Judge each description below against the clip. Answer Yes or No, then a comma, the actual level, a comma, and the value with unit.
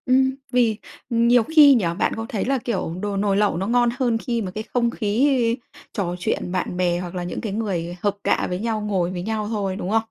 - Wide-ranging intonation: No, average, 4.1 semitones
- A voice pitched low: No, high, 210 Hz